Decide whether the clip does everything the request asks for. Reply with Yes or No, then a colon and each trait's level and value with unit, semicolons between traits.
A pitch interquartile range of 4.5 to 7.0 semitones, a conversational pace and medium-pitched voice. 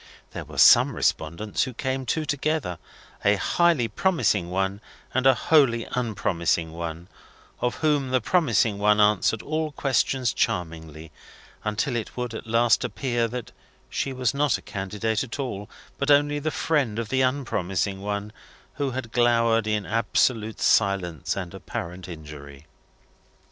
No: average, 5.3 semitones; average, 145 wpm; low, 115 Hz